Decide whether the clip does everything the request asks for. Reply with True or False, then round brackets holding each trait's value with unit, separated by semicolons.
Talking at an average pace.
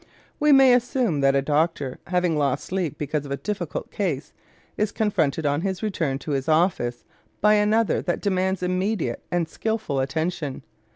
True (165 wpm)